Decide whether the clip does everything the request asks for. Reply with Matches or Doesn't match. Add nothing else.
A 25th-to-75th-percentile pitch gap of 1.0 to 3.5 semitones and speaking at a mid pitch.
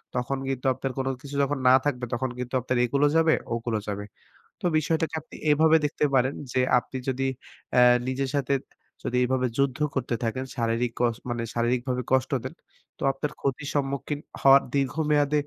Doesn't match